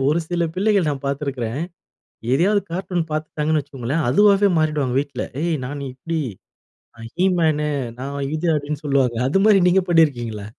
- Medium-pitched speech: Yes, medium, 150 Hz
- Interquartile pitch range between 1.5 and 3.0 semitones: No, average, 4.0 semitones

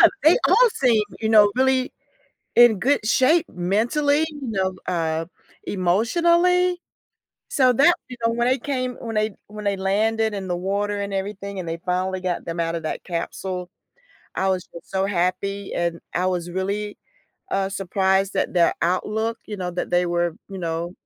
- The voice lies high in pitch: Yes, high, 200 Hz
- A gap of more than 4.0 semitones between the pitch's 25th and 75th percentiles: Yes, average, 4.4 semitones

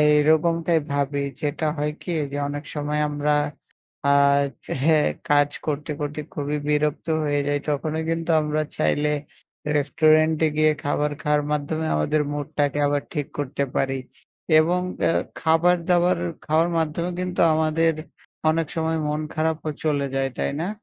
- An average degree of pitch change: No, narrow, 1.7 semitones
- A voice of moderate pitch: Yes, medium, 150 Hz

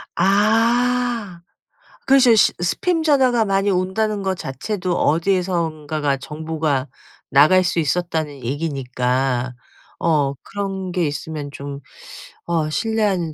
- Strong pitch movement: Yes, wide, 5.7 semitones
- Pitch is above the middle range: No, medium, 175 Hz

